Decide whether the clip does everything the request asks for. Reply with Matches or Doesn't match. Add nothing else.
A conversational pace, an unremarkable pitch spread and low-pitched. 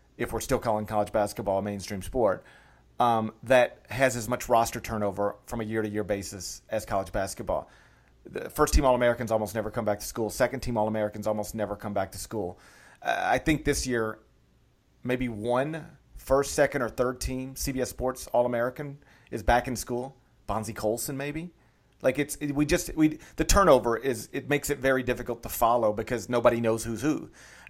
Matches